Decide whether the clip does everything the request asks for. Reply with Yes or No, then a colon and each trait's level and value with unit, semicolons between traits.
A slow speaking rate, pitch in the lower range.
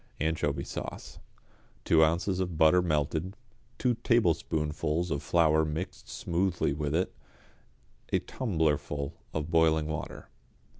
Yes: slow, 110 wpm; very low, 80 Hz